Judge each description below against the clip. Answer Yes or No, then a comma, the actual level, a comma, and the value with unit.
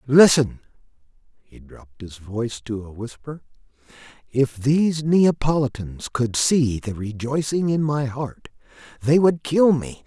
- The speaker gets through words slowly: Yes, slow, 130 wpm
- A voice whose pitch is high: No, low, 135 Hz